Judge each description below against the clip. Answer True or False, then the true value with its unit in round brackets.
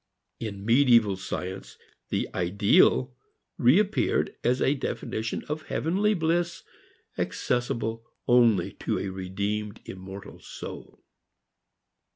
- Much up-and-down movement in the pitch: True (5.9 semitones)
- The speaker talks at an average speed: False (95 wpm)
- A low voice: True (115 Hz)